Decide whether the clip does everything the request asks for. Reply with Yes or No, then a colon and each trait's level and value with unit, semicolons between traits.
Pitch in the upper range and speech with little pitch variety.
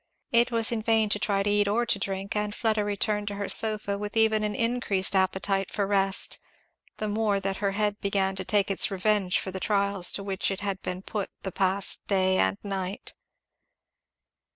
Yes: high, 200 Hz; narrow, 1.6 semitones